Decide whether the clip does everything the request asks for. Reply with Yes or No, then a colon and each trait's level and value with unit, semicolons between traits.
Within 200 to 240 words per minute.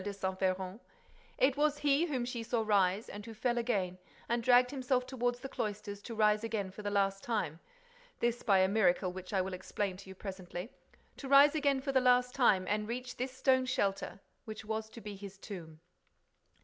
No: average, 190 wpm